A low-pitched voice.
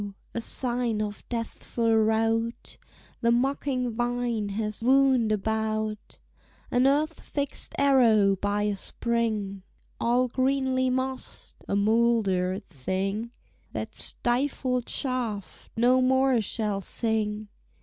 No: high, 230 Hz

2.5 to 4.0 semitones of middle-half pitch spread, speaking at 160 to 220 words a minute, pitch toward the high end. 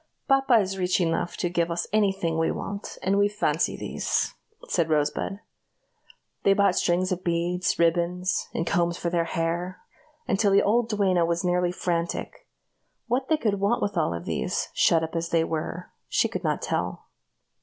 No: average, 2.9 semitones; average, 175 wpm; medium, 180 Hz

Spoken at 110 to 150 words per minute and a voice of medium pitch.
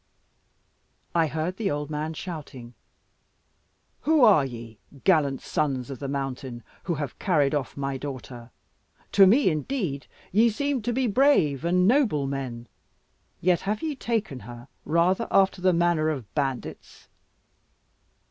Yes: average, 140 wpm; medium, 155 Hz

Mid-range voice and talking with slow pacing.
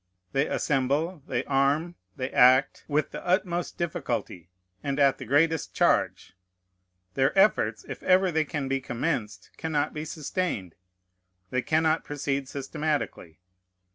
Yes: medium, 145 Hz; slow, 130 wpm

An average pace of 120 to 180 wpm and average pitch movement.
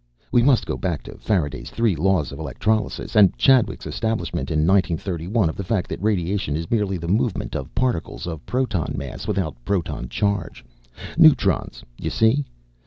Yes: average, 175 wpm; average, 4.9 semitones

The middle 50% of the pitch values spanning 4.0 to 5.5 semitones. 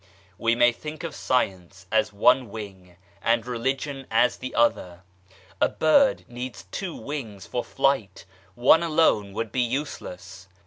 Yes: average, 4.9 semitones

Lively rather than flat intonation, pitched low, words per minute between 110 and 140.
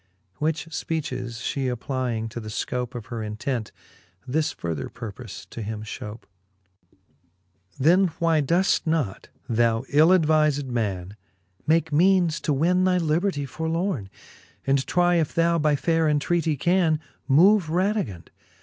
No: wide, 5.9 semitones; medium, 150 Hz; slow, 135 wpm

